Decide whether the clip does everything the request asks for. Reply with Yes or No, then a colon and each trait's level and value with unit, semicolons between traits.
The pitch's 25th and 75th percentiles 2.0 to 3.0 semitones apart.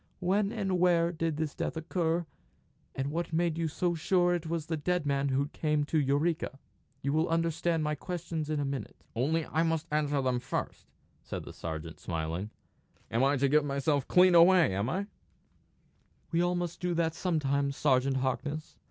No: average, 3.5 semitones